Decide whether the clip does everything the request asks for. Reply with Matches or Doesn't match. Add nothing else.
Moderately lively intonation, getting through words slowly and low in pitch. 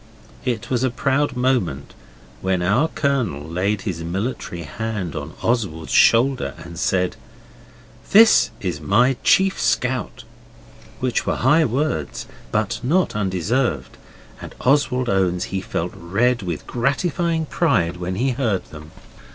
Doesn't match